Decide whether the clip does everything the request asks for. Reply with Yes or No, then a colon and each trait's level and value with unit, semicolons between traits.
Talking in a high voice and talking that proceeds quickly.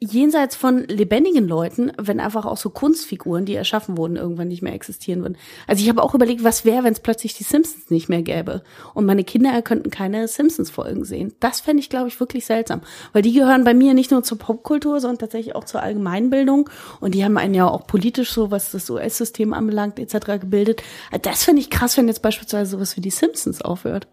Yes: high, 225 Hz; fast, 215 wpm